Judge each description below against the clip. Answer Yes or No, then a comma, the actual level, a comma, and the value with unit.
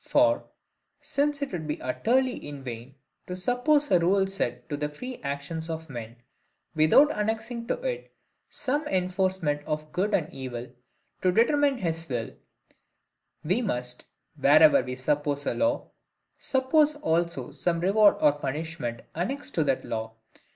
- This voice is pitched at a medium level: Yes, medium, 170 Hz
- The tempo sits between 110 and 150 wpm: Yes, average, 145 wpm